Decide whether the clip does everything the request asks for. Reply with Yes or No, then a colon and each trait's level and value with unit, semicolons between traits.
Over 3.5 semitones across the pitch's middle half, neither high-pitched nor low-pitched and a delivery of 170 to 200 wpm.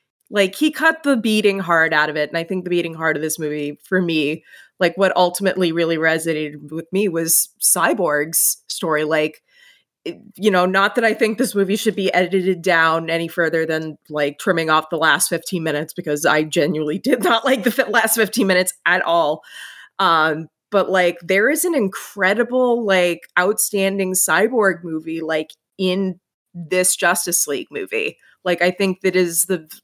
Yes: average, 4.2 semitones; medium, 180 Hz; average, 180 wpm